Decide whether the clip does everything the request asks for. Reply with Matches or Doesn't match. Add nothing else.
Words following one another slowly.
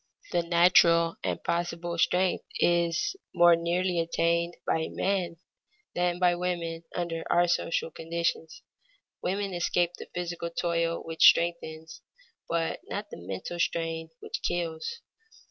Matches